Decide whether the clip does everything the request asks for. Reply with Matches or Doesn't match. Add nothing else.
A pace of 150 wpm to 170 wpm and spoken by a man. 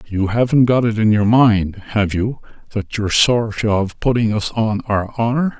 Doesn't match